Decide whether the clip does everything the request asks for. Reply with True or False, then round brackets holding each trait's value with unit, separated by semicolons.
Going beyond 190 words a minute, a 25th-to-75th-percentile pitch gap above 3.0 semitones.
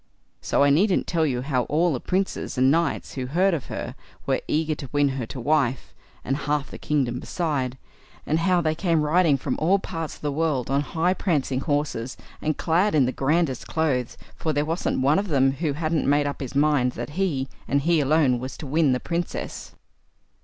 True (205 wpm; 3.4 semitones)